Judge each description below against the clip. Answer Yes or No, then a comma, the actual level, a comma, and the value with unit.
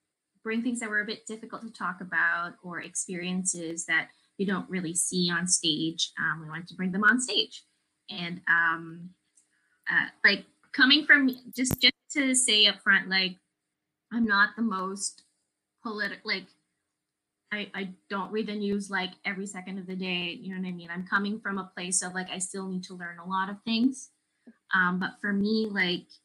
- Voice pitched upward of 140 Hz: Yes, high, 190 Hz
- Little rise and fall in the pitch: No, average, 3.3 semitones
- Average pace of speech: Yes, average, 190 wpm